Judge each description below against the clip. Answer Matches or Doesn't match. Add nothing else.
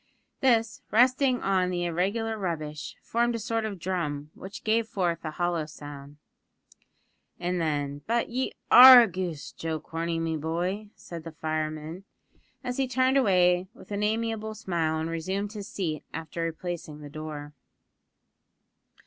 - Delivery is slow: Doesn't match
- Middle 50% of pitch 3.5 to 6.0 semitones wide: Matches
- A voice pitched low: Doesn't match